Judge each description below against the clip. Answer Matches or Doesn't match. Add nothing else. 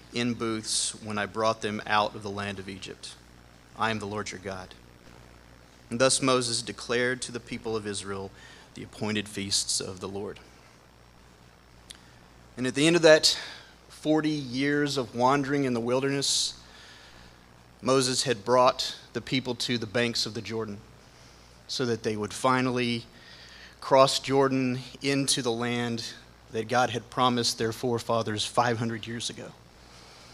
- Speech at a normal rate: Matches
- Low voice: Matches